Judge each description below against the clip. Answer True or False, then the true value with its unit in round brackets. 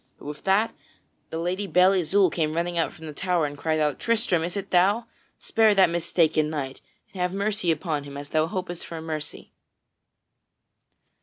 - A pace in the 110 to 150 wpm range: False (180 wpm)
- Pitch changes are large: False (3.6 semitones)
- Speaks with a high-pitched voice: False (170 Hz)